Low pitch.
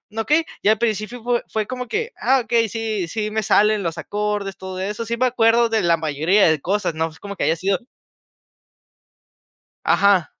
No: high, 210 Hz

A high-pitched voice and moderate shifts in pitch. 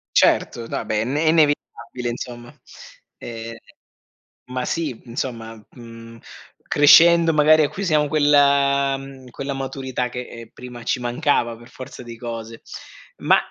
No: low, 130 Hz; average, 3.7 semitones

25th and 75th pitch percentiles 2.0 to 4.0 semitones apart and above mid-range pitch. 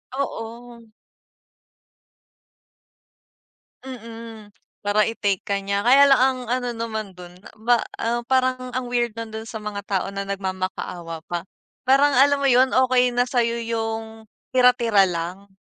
Yes: average, 3.7 semitones; high, 230 Hz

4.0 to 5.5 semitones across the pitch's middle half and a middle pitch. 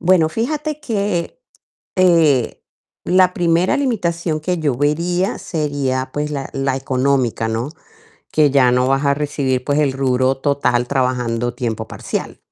Yes: average, 4.7 semitones; medium, 145 Hz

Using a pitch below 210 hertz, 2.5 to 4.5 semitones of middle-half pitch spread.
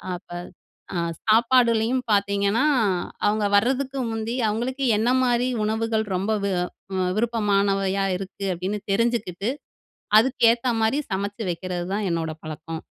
No: high, 215 Hz; average, 3.1 semitones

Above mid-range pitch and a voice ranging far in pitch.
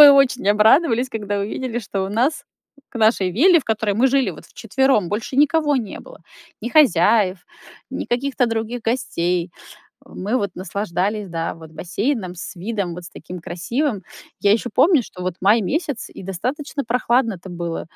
Yes: high, 220 Hz; wide, 5.8 semitones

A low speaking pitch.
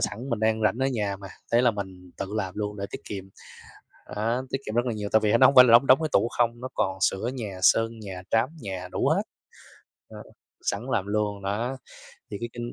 Yes: low, 110 Hz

